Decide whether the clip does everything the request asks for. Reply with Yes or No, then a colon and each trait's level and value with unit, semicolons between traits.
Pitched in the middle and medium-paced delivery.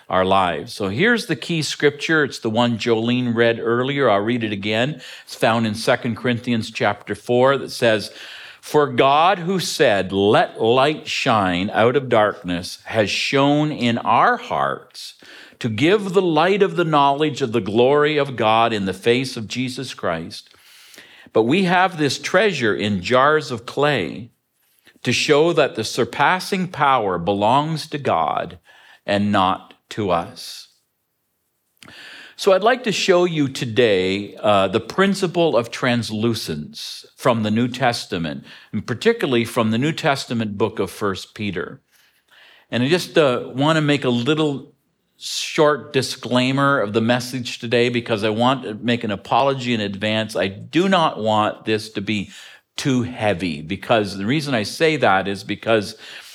No: low, 120 Hz; average, 160 wpm